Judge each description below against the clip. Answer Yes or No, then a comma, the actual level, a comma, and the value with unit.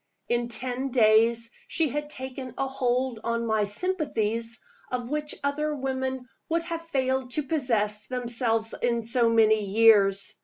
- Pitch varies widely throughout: No, average, 3.0 semitones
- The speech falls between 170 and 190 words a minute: No, average, 145 wpm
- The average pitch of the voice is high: Yes, high, 245 Hz